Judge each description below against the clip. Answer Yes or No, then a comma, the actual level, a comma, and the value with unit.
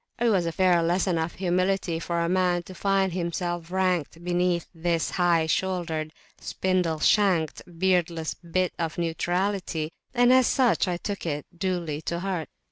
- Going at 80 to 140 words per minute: No, average, 155 wpm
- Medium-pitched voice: Yes, medium, 175 Hz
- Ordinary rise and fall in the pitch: No, narrow, 2.0 semitones